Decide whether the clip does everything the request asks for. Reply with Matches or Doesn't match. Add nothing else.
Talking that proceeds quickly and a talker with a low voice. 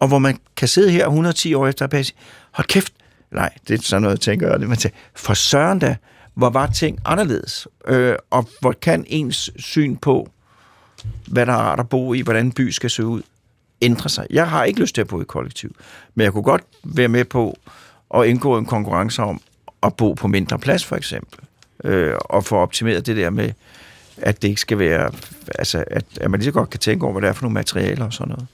Matches